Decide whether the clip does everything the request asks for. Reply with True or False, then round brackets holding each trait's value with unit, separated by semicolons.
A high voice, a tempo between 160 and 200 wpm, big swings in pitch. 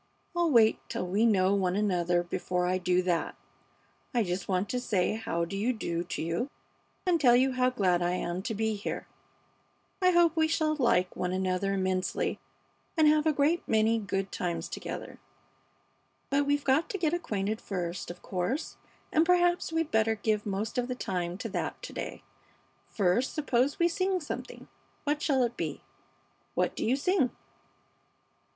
True (220 Hz; 175 wpm; 7.8 semitones)